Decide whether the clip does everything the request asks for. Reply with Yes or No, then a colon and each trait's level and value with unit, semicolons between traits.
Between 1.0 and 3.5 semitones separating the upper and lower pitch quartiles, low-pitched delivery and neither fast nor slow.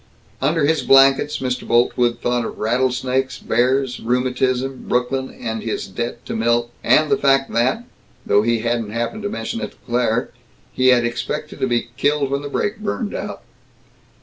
Yes: narrow, 2.6 semitones; low, 125 Hz; average, 170 wpm